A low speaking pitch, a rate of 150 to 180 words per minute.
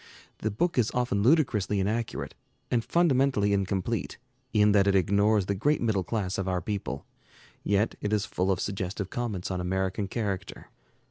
Yes: low, 100 Hz; average, 160 wpm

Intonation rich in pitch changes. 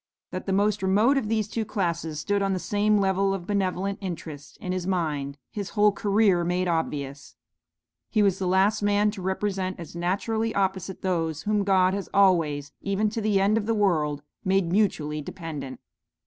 No: average, 3.2 semitones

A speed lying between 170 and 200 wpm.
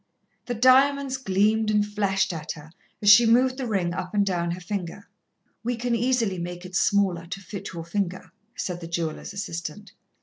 Yes: average, 180 wpm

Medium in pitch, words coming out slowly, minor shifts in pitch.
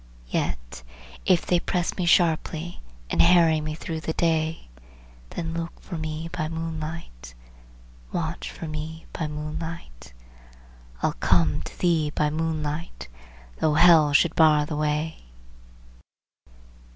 Yes: medium, 160 Hz; slow, 125 wpm; narrow, 1.6 semitones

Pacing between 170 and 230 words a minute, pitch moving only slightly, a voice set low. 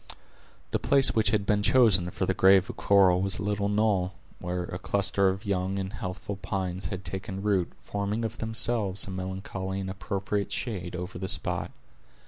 Yes: average, 180 wpm; narrow, 1.6 semitones; very low, 95 Hz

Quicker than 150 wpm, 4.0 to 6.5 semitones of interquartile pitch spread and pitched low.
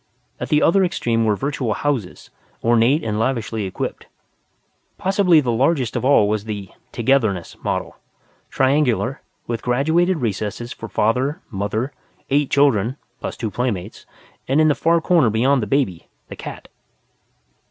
No: average, 140 wpm; average, 4.7 semitones; low, 125 Hz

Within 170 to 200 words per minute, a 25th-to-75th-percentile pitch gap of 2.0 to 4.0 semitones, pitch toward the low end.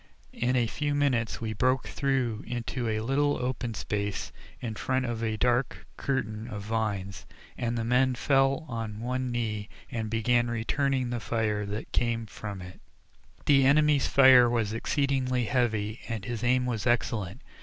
No: average, 160 wpm; average, 2.7 semitones; low, 120 Hz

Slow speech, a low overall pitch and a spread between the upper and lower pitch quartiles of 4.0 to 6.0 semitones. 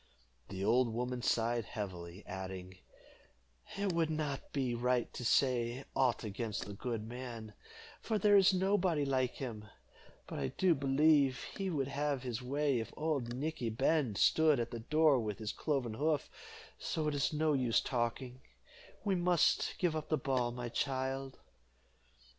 No: average, 160 wpm; low, 130 Hz; average, 4.6 semitones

